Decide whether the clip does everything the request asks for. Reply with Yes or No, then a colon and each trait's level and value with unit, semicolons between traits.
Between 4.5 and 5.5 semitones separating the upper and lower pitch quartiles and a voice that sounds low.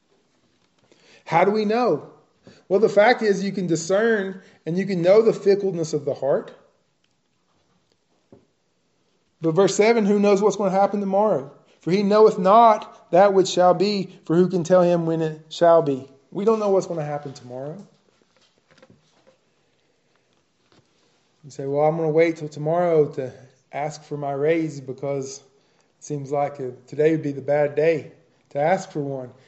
No: average, 5.2 semitones; medium, 170 Hz